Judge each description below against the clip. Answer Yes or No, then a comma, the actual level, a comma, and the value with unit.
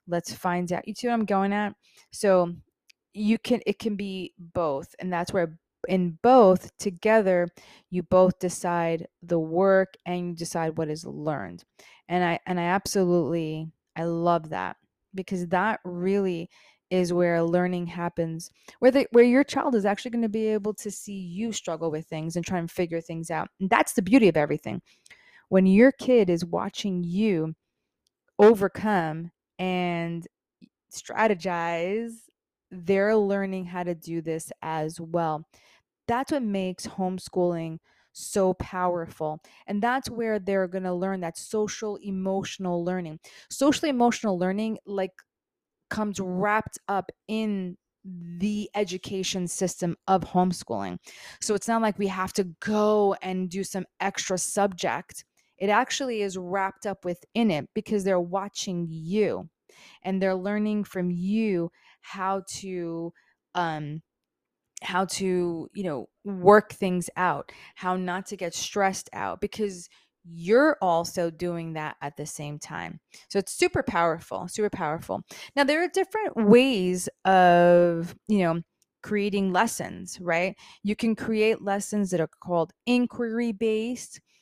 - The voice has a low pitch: No, high, 190 Hz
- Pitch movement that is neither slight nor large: Yes, average, 3.3 semitones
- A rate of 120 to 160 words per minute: Yes, average, 145 wpm